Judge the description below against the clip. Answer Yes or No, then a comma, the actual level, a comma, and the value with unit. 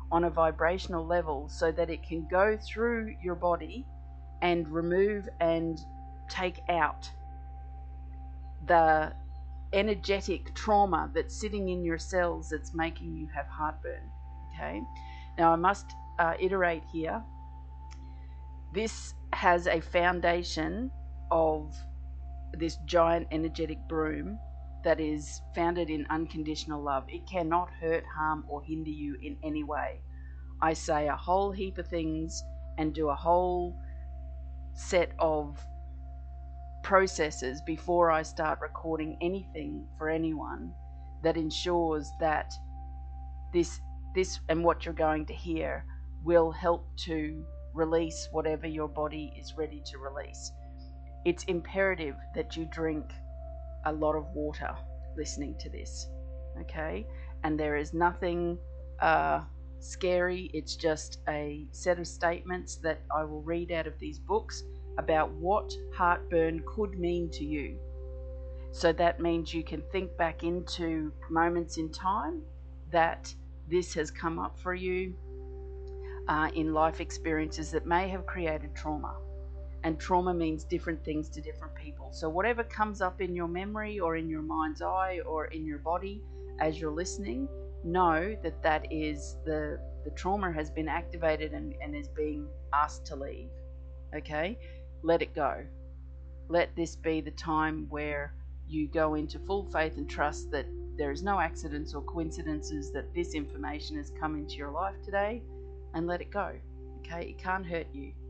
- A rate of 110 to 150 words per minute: Yes, average, 145 wpm